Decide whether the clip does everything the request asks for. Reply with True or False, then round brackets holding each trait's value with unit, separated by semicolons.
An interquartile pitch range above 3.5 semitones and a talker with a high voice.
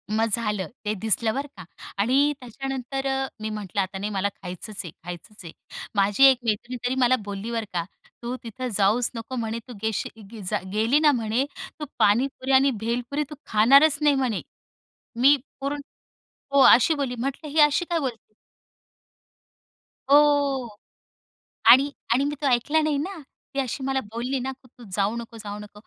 True (4.2 semitones; 245 Hz)